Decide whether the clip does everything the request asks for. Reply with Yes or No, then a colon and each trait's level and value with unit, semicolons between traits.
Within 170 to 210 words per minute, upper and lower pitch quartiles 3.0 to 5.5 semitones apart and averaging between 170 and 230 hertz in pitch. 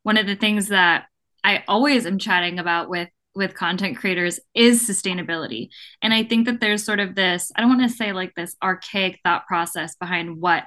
Yes: fast, 205 wpm; average, 3.4 semitones; high, 190 Hz